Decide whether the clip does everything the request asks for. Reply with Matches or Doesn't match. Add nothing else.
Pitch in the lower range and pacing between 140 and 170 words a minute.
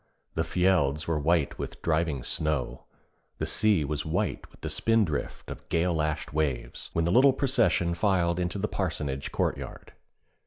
Matches